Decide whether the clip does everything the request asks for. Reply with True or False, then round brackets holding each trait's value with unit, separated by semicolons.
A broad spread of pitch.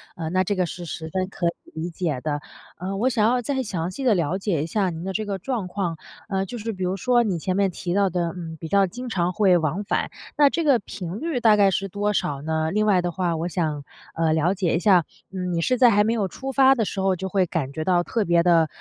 False (3.6 semitones)